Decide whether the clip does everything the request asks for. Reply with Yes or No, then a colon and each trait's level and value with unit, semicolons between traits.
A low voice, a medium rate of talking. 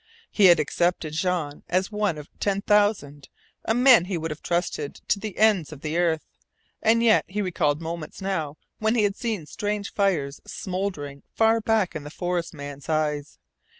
No: medium, 180 Hz; average, 180 wpm